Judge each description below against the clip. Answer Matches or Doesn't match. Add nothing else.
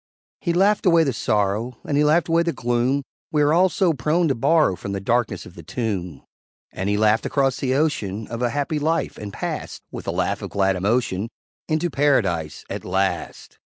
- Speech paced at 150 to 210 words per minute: Matches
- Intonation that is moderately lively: Doesn't match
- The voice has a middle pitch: Doesn't match